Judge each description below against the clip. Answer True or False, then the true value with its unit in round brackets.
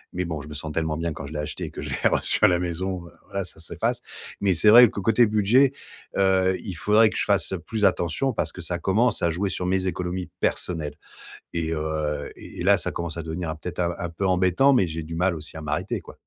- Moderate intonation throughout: True (3.3 semitones)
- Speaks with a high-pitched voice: False (90 Hz)